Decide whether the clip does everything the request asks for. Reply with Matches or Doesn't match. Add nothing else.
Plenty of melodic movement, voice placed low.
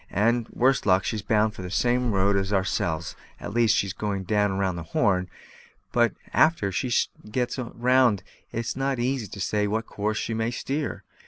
Doesn't match